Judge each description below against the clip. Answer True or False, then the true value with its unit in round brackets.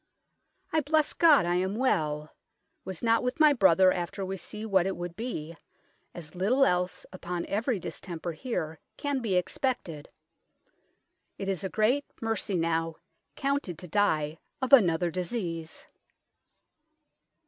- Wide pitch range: True (5.8 semitones)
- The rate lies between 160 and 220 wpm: False (135 wpm)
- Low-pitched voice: False (190 Hz)